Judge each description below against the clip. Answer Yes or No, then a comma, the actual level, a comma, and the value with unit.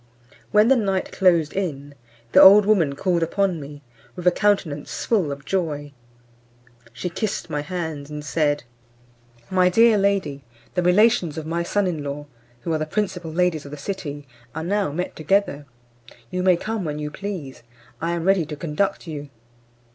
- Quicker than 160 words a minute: Yes, average, 170 wpm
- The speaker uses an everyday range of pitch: Yes, average, 4.6 semitones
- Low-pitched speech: No, medium, 170 Hz